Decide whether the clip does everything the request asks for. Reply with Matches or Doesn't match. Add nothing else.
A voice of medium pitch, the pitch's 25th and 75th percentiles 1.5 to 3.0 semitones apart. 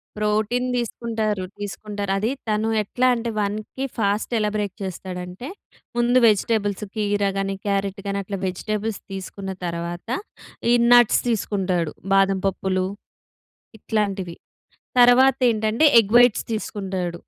Doesn't match